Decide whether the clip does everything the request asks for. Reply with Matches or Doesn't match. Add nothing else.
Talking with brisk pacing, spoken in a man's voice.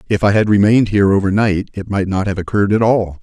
Matches